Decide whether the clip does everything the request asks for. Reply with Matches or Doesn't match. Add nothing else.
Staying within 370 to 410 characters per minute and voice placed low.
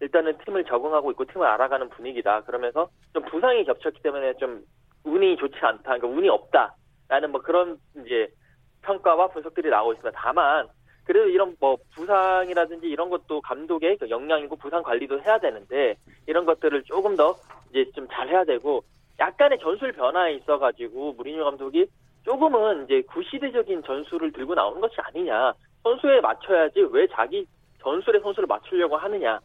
Doesn't match